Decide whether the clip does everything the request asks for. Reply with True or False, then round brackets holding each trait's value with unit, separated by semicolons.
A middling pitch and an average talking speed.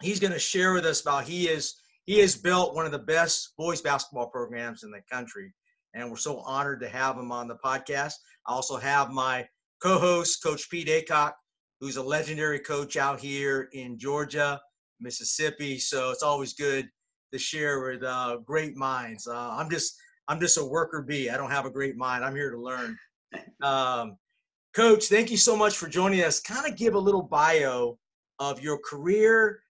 True (145 Hz; 190 wpm)